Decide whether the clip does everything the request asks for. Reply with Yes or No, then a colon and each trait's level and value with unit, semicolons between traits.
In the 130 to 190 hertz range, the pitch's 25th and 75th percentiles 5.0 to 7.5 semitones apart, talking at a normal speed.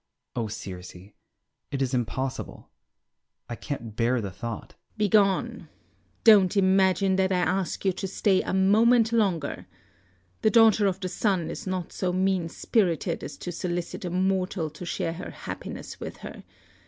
Yes: medium, 185 Hz; average, 5.3 semitones; average, 155 wpm